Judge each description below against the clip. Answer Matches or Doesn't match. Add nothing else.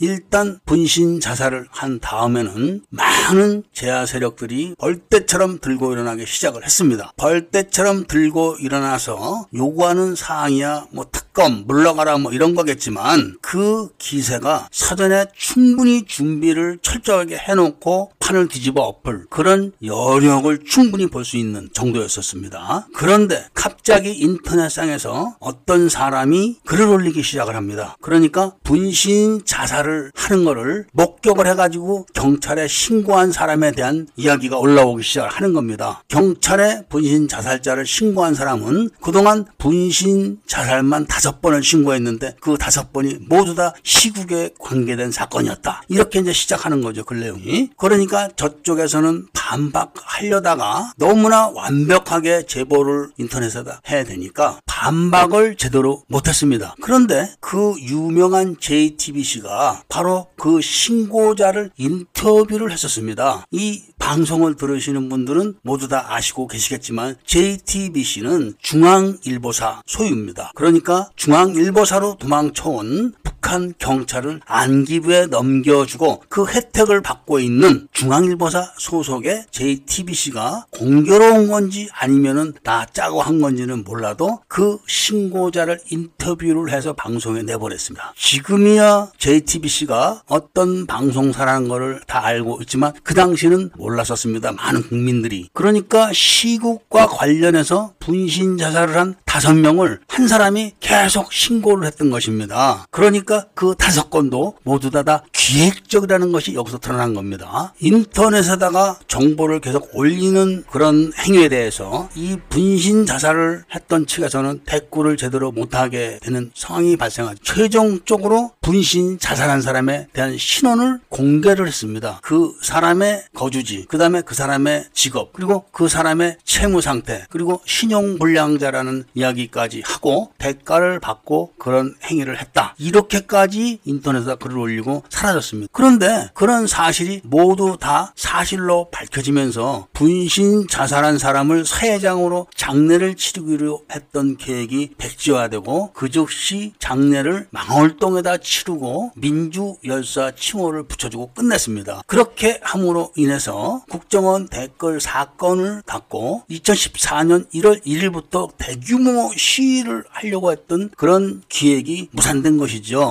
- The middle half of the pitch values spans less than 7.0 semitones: Matches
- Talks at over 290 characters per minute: Matches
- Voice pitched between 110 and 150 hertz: Doesn't match